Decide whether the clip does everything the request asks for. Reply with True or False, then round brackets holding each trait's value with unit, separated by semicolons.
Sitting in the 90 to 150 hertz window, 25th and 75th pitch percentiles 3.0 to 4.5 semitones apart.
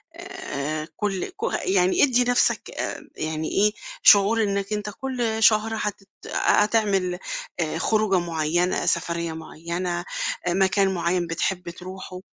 False (190 Hz; 3.7 semitones)